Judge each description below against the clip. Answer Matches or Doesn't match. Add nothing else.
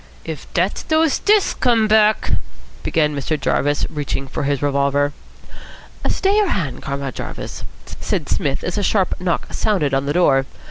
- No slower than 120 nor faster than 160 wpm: Matches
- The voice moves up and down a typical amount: Doesn't match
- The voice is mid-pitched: Matches